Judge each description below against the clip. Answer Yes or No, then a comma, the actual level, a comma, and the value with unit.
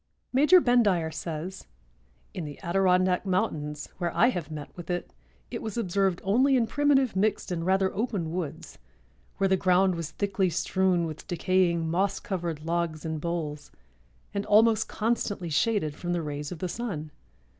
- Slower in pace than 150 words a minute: No, average, 160 wpm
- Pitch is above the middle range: No, medium, 180 Hz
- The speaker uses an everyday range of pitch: Yes, average, 3.5 semitones